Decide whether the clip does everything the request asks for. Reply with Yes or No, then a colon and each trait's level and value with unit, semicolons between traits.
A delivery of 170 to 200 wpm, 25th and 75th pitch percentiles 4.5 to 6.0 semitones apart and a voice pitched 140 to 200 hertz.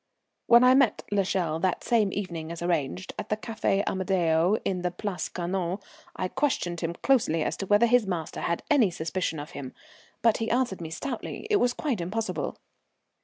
Yes: average, 180 wpm; average, 4.9 semitones; high, 190 Hz